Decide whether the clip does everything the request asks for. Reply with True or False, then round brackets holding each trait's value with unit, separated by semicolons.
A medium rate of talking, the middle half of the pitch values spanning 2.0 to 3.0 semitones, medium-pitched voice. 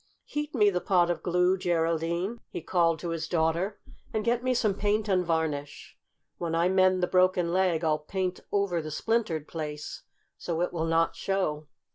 True (180 wpm; 2.7 semitones; 175 Hz)